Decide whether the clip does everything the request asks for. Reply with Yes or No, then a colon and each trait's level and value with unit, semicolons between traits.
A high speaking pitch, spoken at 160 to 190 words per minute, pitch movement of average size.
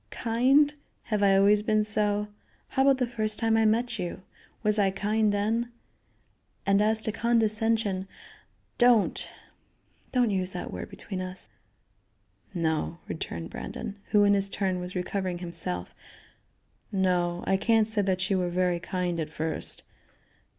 No: high, 205 Hz; average, 145 wpm; average, 3.2 semitones